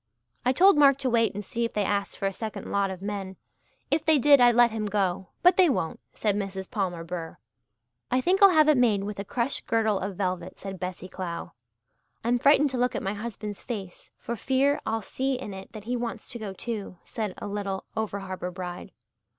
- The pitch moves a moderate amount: Yes, average, 4.4 semitones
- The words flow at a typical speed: No, fast, 220 wpm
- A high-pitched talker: Yes, high, 210 Hz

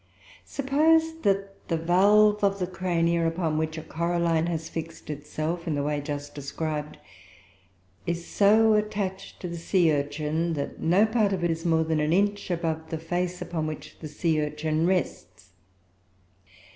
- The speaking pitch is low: No, medium, 170 Hz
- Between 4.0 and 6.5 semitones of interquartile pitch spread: No, average, 3.4 semitones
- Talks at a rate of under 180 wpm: Yes, average, 160 wpm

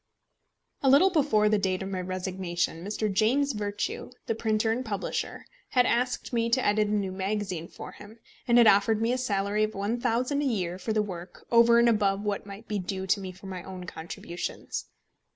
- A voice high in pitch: Yes, high, 210 Hz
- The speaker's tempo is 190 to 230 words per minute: Yes, average, 200 wpm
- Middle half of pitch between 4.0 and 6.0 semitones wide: No, average, 3.4 semitones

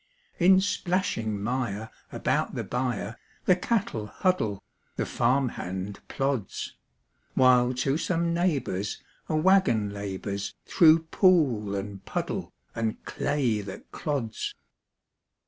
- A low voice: Yes, low, 125 Hz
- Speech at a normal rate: No, slow, 110 wpm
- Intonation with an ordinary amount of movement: No, wide, 7.9 semitones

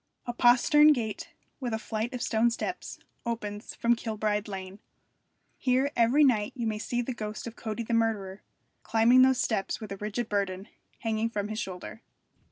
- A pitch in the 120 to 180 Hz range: No, high, 225 Hz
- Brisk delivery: No, average, 175 wpm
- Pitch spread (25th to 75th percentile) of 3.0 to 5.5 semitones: No, narrow, 2.4 semitones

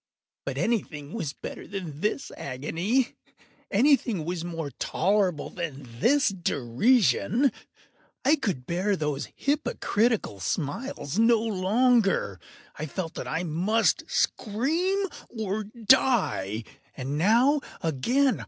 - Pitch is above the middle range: Yes, high, 195 Hz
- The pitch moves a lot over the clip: Yes, wide, 7.7 semitones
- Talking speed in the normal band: No, slow, 105 wpm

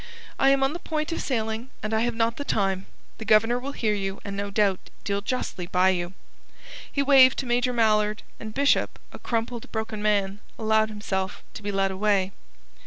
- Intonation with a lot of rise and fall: No, average, 3.4 semitones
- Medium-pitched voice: No, high, 220 Hz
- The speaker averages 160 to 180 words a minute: No, average, 195 wpm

